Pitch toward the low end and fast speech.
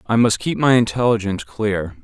No: low, 105 Hz; average, 175 wpm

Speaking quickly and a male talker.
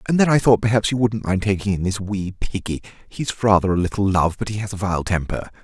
Yes: fast, 255 wpm; male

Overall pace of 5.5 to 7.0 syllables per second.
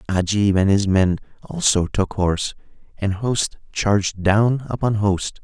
No: 4.1 syllables/s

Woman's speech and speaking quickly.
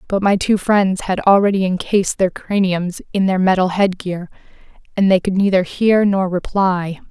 No: female; average, 170 wpm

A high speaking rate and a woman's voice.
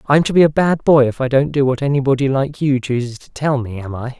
No: fast, 285 wpm; male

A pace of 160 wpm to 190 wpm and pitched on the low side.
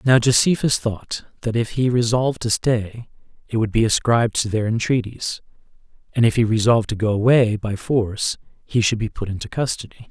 Yes: average, 185 wpm; low, 115 Hz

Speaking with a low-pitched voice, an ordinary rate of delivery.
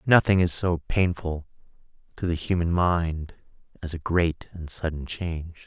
Yes: very low, 85 Hz; average, 150 wpm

